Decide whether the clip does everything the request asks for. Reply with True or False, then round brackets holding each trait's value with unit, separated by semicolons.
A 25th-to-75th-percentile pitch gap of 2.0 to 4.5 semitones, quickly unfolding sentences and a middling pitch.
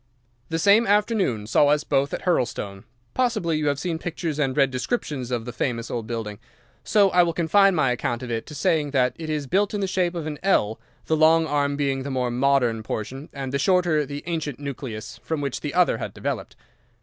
False (5.1 semitones; 215 wpm; 145 Hz)